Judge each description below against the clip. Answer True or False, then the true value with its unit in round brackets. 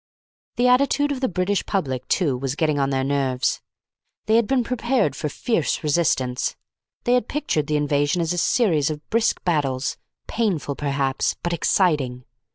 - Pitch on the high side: False (155 Hz)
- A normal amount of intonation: False (8.1 semitones)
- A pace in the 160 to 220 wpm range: True (165 wpm)